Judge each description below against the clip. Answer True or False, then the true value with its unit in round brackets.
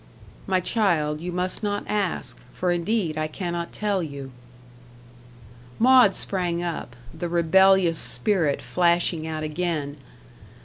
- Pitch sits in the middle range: True (175 Hz)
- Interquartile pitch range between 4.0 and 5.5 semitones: False (3.2 semitones)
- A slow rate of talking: True (120 wpm)